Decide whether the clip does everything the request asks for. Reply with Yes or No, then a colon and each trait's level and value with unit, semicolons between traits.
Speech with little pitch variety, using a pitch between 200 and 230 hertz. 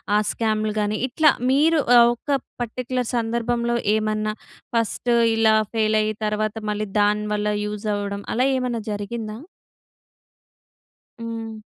Yes: narrow, 2.0 semitones; high, 220 Hz